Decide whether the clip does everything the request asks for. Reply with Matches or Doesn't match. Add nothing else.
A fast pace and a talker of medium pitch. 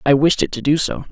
Matches